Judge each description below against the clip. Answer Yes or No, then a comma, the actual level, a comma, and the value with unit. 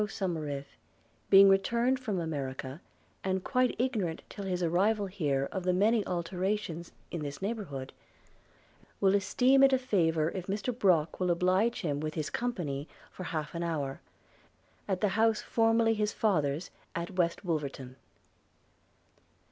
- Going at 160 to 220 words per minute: No, average, 145 wpm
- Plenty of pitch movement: No, average, 5.0 semitones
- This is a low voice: No, medium, 185 Hz